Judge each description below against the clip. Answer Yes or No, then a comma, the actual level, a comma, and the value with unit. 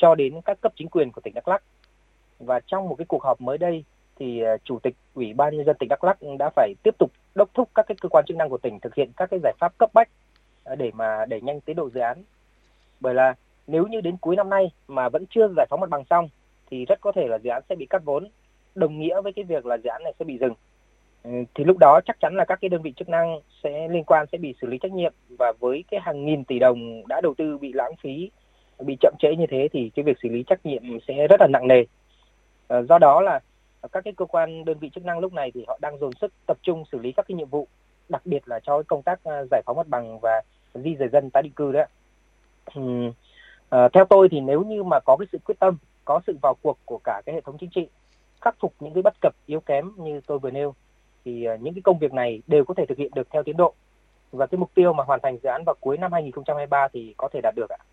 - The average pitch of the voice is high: No, medium, 155 Hz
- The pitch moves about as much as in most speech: No, wide, 5.9 semitones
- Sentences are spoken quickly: Yes, fast, 270 wpm